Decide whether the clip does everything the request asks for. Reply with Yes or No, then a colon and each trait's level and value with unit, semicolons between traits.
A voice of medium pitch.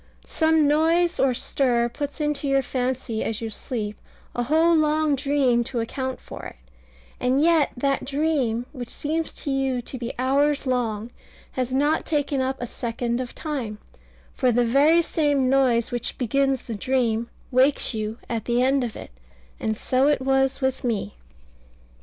No: very high, 265 Hz